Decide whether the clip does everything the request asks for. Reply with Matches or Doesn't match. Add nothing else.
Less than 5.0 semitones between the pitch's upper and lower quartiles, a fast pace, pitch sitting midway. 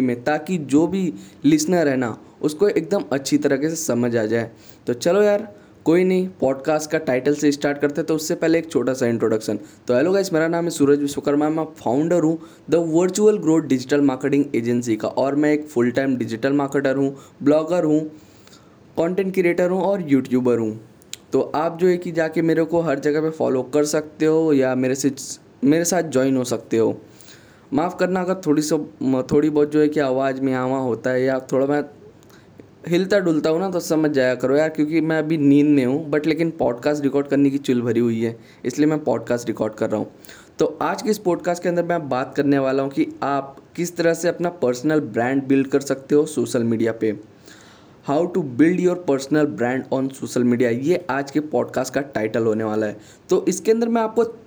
Matches